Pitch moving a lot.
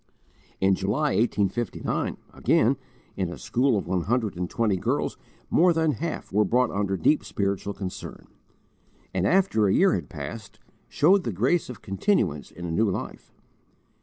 Yes: wide, 5.7 semitones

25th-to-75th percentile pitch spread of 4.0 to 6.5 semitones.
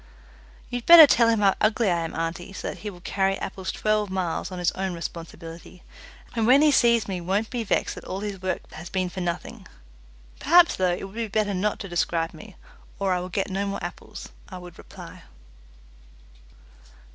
No: average, 3.2 semitones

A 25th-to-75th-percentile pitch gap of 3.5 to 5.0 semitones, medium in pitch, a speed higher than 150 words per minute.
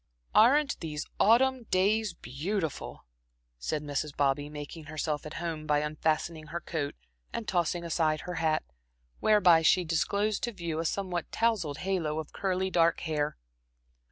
No: average, 4.0 semitones; medium, 165 Hz; average, 145 wpm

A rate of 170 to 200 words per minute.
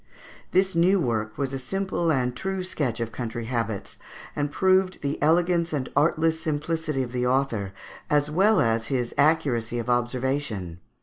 No: average, 160 wpm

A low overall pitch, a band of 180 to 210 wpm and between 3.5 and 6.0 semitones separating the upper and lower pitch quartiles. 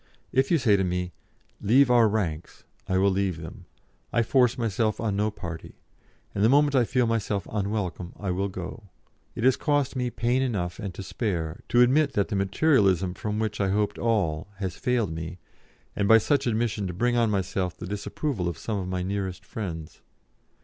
Yes: low, 105 Hz; average, 190 wpm; average, 4.4 semitones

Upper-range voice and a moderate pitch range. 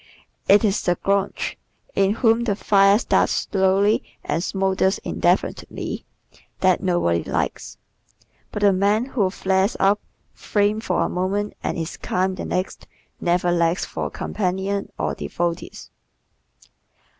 No: high, 195 Hz; narrow, 2.1 semitones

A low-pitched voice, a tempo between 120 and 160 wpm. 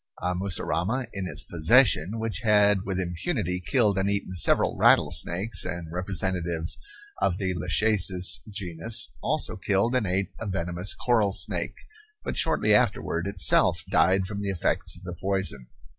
Yes: very low, 95 Hz; average, 145 wpm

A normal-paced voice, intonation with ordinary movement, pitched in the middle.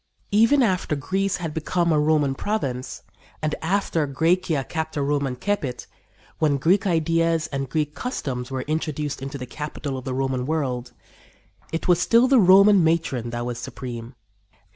Yes: average, 155 wpm; average, 4.7 semitones; medium, 155 Hz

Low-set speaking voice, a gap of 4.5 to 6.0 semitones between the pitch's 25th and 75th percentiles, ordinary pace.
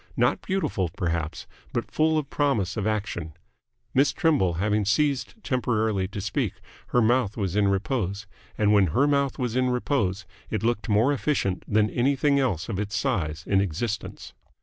Yes: low, 110 Hz; average, 5.2 semitones; average, 165 wpm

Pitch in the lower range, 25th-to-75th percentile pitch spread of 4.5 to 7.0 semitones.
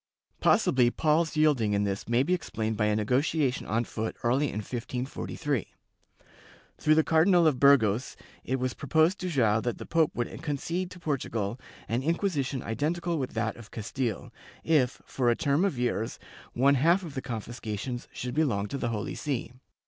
Yes: low, 130 Hz; average, 5.2 semitones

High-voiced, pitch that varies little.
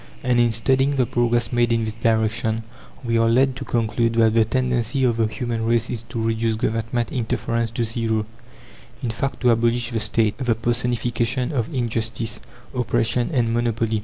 No: low, 115 Hz; narrow, 1.3 semitones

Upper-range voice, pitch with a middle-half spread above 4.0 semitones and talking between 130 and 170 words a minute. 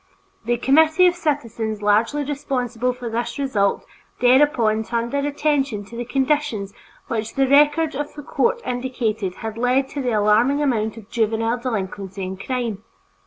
Yes: high, 245 Hz; average, 4.4 semitones; average, 155 wpm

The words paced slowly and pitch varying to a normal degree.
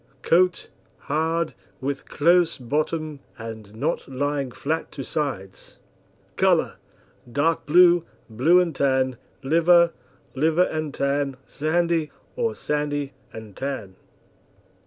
Yes: slow, 105 wpm; average, 3.7 semitones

